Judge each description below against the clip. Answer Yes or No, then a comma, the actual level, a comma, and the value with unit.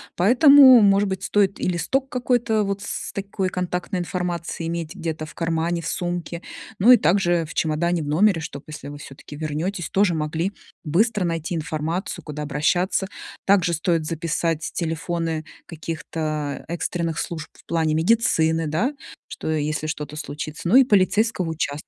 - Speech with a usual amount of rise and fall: Yes, average, 3.5 semitones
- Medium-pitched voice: Yes, medium, 170 Hz